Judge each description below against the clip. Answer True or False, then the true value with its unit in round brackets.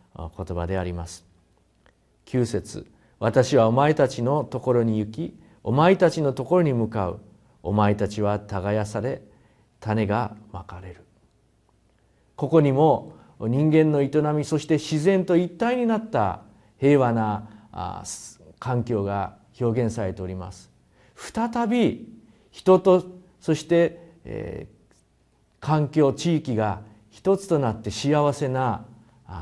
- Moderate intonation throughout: False (6.7 semitones)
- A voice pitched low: True (120 Hz)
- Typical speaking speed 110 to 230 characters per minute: True (215 characters per minute)